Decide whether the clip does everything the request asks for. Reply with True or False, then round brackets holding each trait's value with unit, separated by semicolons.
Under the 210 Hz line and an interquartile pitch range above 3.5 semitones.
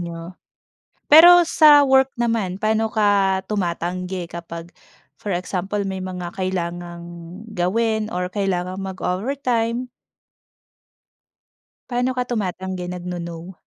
True (190 Hz; 4.2 semitones)